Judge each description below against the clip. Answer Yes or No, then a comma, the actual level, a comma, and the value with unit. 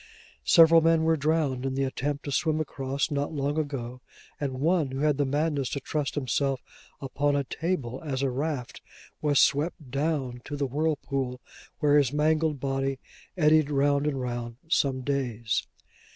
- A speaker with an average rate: Yes, average, 165 wpm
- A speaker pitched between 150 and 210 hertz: No, medium, 140 Hz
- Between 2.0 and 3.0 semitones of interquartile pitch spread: Yes, narrow, 2.4 semitones